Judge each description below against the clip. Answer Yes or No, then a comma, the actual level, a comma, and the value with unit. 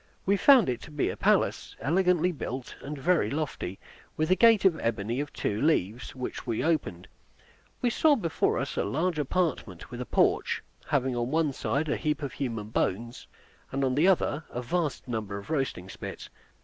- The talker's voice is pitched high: No, medium, 140 Hz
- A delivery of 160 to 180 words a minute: No, average, 190 wpm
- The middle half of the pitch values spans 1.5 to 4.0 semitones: No, wide, 5.6 semitones